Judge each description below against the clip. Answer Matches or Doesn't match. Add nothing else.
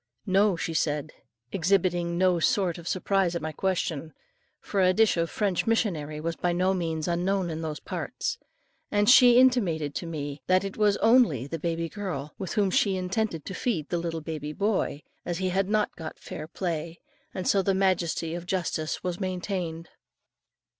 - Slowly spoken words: Doesn't match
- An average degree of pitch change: Matches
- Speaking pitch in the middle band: Matches